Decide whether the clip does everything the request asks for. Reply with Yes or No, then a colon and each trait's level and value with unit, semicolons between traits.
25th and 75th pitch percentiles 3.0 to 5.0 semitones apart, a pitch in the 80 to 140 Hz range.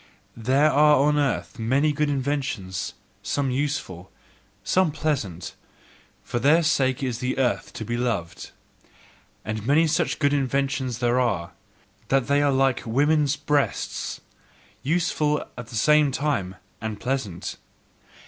Yes: average, 4.1 semitones; low, 135 Hz